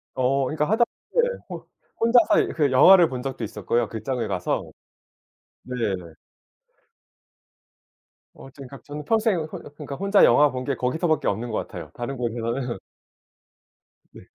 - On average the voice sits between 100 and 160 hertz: Yes, low, 135 Hz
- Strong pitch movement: No, average, 4.6 semitones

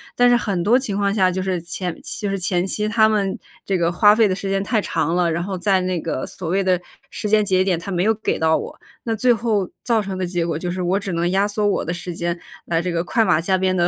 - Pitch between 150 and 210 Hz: Yes, high, 190 Hz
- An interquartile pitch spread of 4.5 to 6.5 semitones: No, average, 2.8 semitones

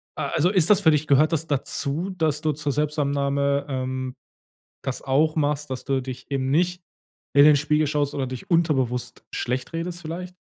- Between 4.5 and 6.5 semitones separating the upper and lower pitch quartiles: No, average, 2.8 semitones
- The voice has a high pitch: No, medium, 145 Hz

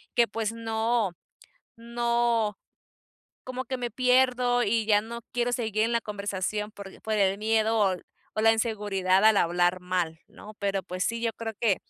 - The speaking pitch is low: No, high, 220 Hz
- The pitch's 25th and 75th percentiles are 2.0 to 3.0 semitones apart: Yes, average, 2.7 semitones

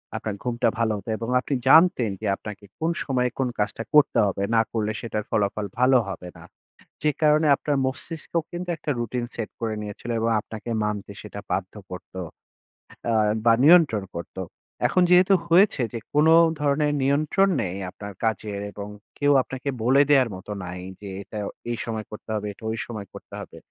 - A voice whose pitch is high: No, low, 115 Hz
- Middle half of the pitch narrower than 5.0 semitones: No, wide, 5.5 semitones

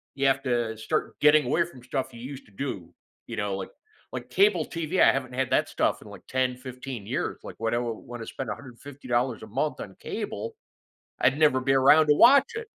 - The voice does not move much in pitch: No, average, 3.4 semitones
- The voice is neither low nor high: No, low, 130 Hz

